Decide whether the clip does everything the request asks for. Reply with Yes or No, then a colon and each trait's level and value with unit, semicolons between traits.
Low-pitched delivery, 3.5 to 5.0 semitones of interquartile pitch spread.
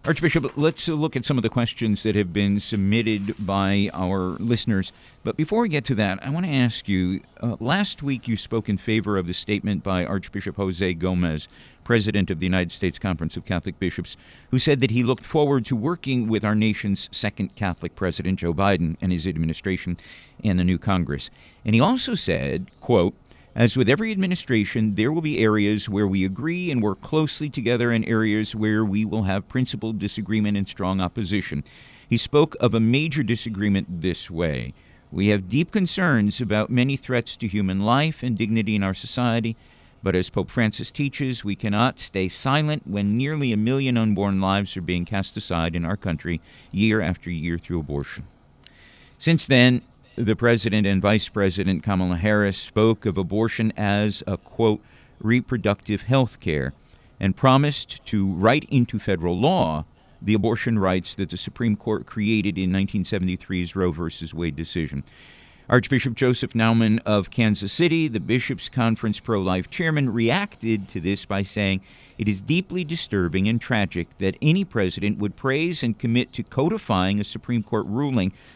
Yes: low, 105 Hz; average, 4.4 semitones